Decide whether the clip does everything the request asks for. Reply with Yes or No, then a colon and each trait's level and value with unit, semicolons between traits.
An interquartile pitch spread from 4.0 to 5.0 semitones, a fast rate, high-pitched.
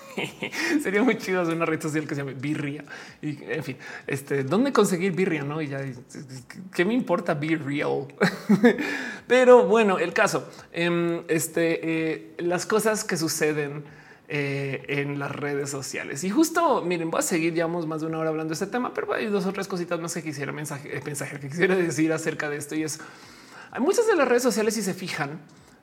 No: average, 4.6 semitones; fast, 195 wpm; medium, 160 Hz